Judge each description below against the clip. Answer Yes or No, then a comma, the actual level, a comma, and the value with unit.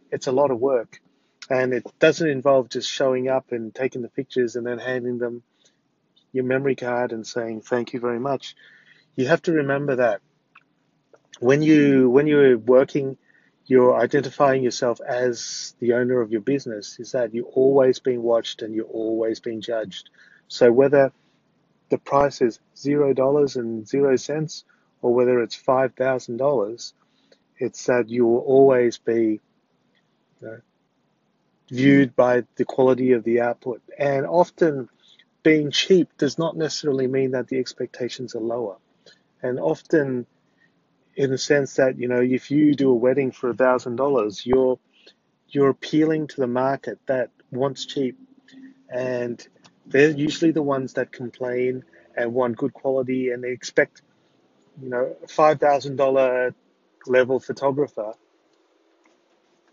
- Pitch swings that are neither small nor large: No, narrow, 2.2 semitones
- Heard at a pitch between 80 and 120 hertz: No, low, 130 Hz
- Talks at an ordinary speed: Yes, average, 145 wpm